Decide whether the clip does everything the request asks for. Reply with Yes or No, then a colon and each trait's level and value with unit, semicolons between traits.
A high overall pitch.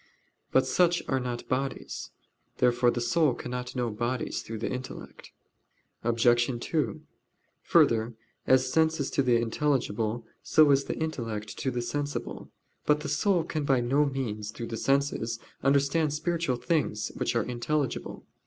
No: low, 130 Hz